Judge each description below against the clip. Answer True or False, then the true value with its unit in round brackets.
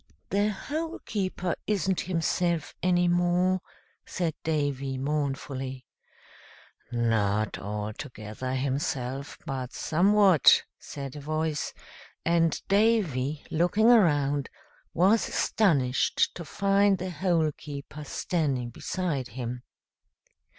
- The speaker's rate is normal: False (95 wpm)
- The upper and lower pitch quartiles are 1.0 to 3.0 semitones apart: False (5.6 semitones)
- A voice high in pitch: False (155 Hz)